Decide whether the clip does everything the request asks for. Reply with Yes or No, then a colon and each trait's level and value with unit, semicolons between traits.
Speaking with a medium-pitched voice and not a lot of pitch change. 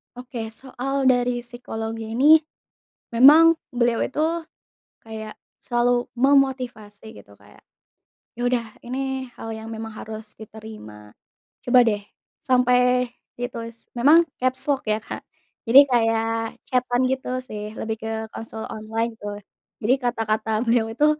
No: high, 235 Hz; narrow, 2.3 semitones